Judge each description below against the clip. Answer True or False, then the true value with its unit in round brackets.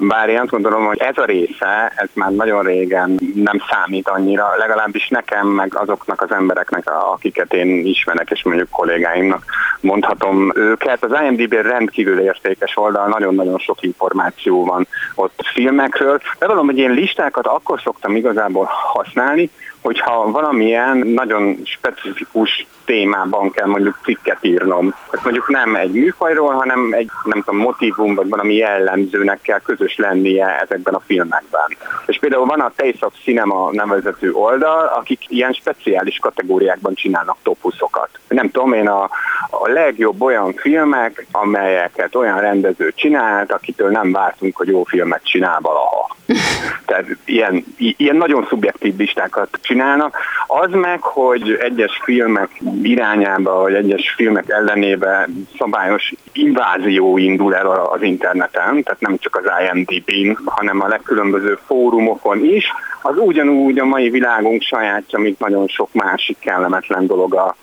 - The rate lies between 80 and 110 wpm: False (140 wpm)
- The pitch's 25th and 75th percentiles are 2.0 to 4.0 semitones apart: False (5.5 semitones)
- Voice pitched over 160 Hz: False (105 Hz)